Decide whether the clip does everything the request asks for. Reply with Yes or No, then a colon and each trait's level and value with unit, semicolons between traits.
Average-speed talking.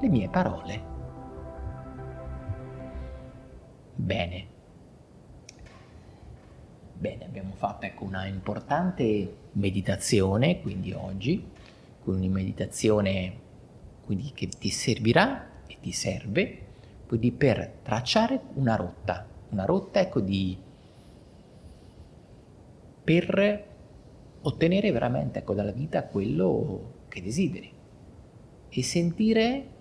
No: slow, 85 wpm